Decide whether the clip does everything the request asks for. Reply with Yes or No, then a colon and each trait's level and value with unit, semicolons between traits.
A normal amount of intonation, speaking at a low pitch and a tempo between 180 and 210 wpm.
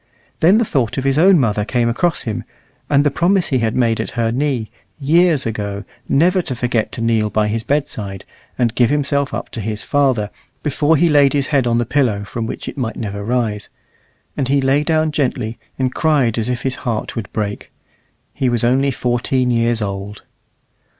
Yes: average, 4.1 semitones; low, 125 Hz; average, 195 wpm